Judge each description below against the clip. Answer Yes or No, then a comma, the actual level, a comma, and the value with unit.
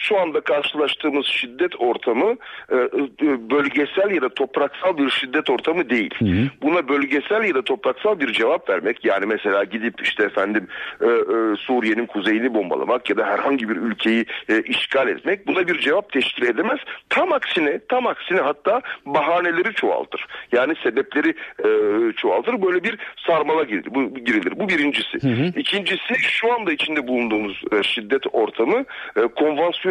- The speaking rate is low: No, average, 130 wpm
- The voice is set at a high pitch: Yes, high, 195 Hz